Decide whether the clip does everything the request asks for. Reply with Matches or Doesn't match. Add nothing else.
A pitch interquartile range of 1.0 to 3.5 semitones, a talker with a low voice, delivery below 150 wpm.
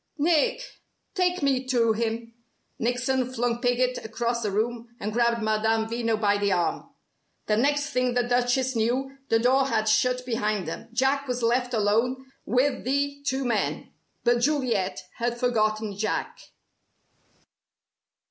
Doesn't match